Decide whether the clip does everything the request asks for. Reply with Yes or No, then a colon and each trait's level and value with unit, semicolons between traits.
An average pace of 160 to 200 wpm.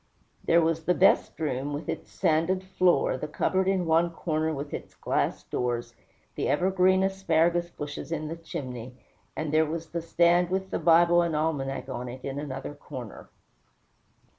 Yes: average, 170 wpm